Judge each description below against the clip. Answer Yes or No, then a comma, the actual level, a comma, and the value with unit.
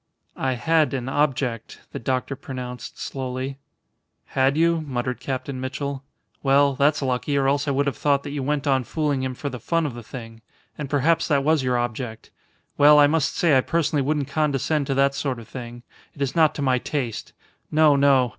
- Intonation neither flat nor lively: No, narrow, 2.3 semitones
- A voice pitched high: No, medium, 140 Hz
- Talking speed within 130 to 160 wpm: No, average, 200 wpm